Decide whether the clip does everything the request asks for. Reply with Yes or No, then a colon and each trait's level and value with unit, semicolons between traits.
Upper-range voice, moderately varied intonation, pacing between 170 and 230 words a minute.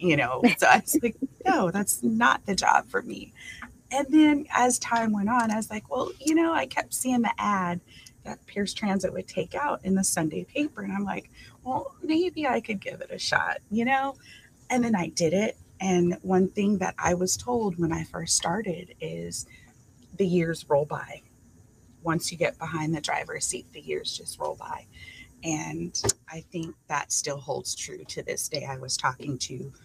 No: high, 195 Hz; wide, 7.2 semitones; average, 200 wpm